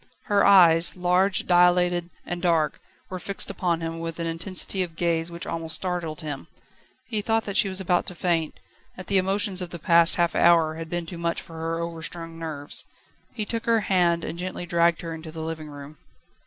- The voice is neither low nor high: Yes, medium, 170 Hz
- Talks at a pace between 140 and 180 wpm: No, average, 200 wpm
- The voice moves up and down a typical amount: No, narrow, 1.9 semitones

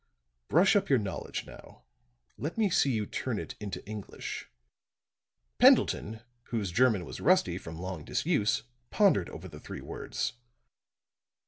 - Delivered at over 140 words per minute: No, slow, 135 wpm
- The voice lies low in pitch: Yes, low, 110 Hz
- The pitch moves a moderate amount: No, wide, 6.9 semitones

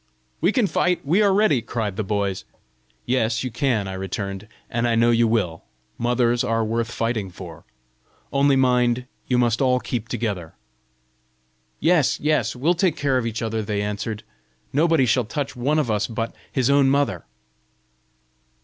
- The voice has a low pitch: Yes, low, 120 Hz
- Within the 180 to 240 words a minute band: No, average, 165 wpm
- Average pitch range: Yes, average, 4.2 semitones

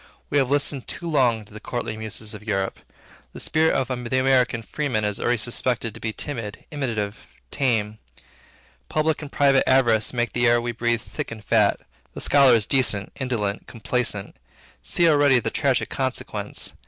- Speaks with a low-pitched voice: Yes, low, 120 Hz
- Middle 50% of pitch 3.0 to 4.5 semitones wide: Yes, average, 3.6 semitones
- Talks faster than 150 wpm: Yes, average, 170 wpm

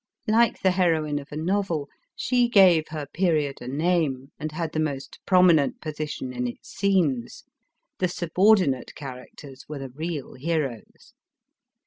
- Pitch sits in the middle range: Yes, medium, 155 Hz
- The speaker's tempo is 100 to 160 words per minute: Yes, average, 140 wpm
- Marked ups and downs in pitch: No, average, 4.6 semitones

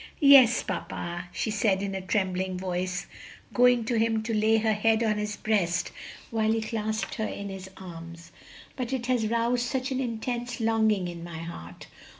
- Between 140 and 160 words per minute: No, average, 175 wpm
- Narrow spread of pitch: No, average, 3.6 semitones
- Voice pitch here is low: No, high, 215 Hz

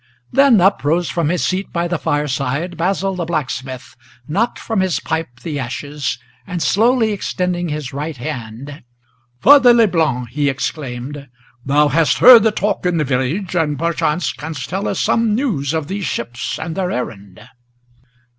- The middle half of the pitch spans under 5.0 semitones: No, wide, 5.5 semitones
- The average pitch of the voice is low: No, medium, 160 Hz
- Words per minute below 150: No, average, 160 wpm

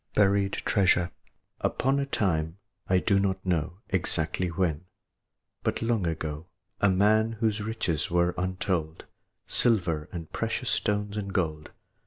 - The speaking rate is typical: No, slow, 130 wpm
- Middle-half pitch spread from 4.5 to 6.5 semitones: No, average, 3.7 semitones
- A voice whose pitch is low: Yes, very low, 95 Hz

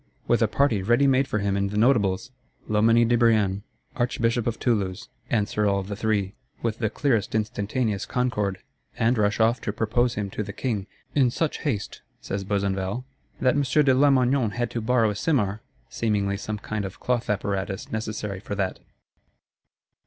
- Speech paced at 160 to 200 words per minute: Yes, average, 165 wpm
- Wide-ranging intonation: No, average, 3.2 semitones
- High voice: No, low, 110 Hz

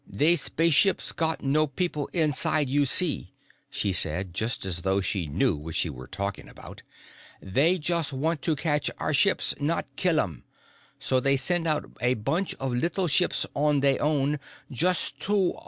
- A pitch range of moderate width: No, wide, 5.9 semitones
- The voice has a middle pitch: Yes, medium, 145 Hz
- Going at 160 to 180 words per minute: Yes, average, 170 wpm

